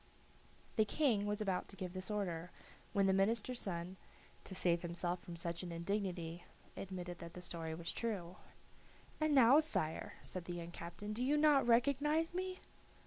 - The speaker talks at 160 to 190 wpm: Yes, average, 170 wpm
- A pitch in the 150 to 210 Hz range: Yes, high, 190 Hz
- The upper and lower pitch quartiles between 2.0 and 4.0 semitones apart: No, average, 5.3 semitones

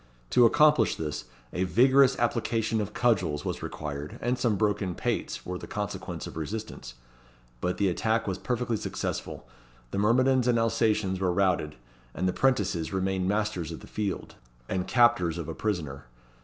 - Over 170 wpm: No, average, 160 wpm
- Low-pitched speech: Yes, low, 105 Hz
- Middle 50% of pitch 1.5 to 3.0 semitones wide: No, average, 4.4 semitones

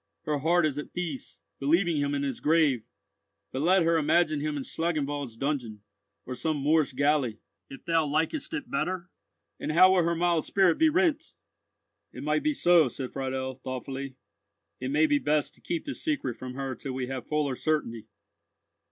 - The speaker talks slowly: No, average, 180 wpm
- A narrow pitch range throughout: No, average, 4.1 semitones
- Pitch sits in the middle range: Yes, medium, 150 Hz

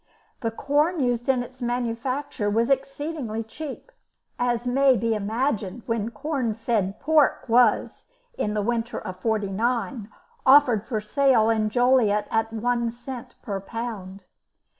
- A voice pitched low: No, high, 235 Hz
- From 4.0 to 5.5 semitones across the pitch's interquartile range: No, average, 3.1 semitones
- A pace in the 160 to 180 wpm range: No, slow, 135 wpm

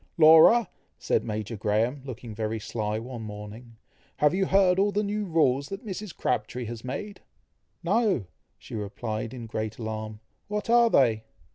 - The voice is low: Yes, low, 125 Hz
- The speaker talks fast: No, average, 155 wpm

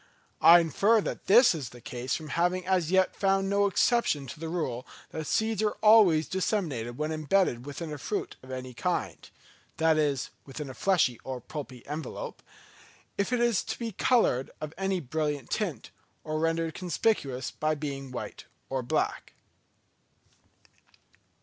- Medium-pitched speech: Yes, medium, 160 Hz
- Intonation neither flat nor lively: No, wide, 6.0 semitones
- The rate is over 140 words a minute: Yes, average, 155 wpm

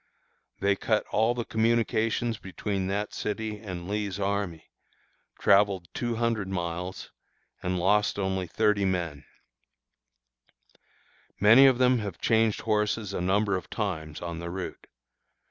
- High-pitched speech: No, low, 100 Hz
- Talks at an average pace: No, slow, 130 wpm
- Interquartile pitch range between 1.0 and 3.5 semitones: Yes, average, 3.0 semitones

